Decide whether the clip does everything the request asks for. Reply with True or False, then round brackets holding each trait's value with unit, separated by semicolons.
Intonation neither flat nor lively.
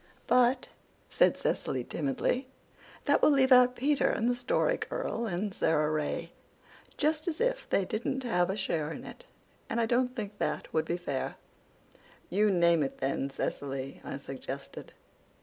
False (8.3 semitones)